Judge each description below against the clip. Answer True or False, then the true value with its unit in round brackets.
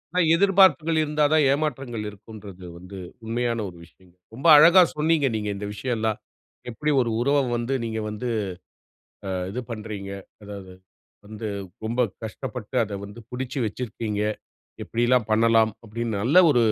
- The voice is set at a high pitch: False (115 Hz)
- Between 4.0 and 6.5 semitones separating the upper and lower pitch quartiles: True (4.3 semitones)